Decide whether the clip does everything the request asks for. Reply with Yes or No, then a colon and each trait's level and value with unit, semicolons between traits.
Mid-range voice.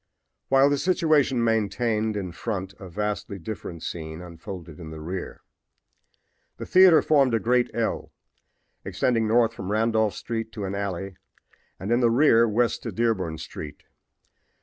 No: low, 110 Hz